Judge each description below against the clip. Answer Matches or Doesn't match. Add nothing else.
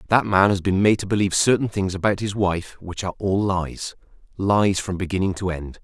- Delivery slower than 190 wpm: Doesn't match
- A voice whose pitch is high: Doesn't match